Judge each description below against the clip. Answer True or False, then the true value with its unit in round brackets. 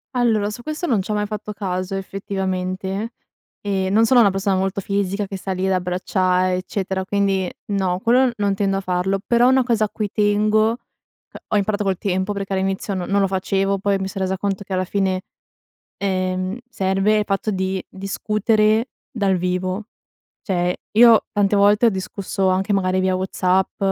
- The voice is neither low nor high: False (195 Hz)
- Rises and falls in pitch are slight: True (1.8 semitones)